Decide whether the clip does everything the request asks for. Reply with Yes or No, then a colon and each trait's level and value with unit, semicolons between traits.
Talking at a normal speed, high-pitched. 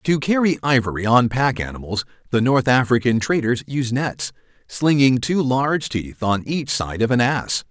No: average, 170 wpm; low, 125 Hz